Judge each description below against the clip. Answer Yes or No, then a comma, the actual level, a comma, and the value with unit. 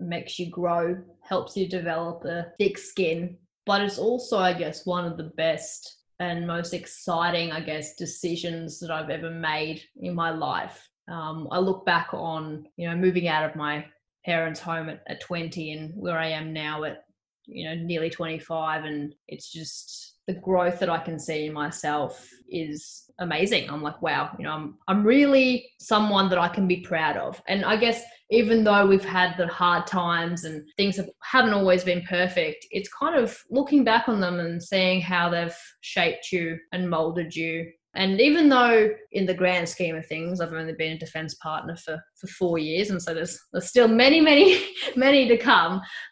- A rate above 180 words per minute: Yes, average, 190 wpm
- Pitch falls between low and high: Yes, medium, 175 Hz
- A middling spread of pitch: Yes, average, 3.0 semitones